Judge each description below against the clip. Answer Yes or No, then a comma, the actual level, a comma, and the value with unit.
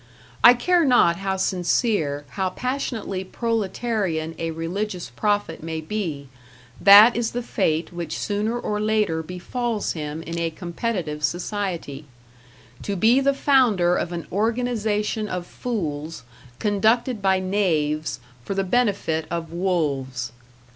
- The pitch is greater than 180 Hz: Yes, high, 190 Hz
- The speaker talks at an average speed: No, slow, 125 wpm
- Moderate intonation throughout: Yes, average, 5.0 semitones